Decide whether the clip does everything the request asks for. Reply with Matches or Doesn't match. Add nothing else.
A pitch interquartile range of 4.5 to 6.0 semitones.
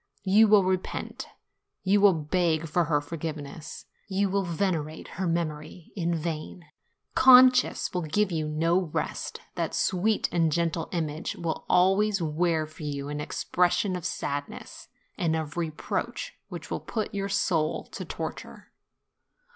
Doesn't match